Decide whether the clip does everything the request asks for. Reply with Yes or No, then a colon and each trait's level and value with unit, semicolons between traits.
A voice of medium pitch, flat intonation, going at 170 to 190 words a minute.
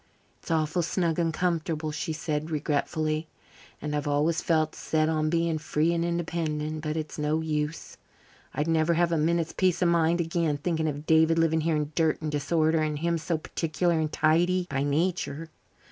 Yes: medium, 160 Hz; narrow, 1.6 semitones; average, 180 wpm